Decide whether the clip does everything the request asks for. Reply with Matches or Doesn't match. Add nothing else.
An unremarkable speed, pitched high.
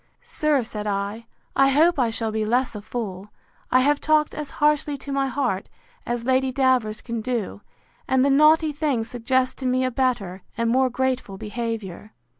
Matches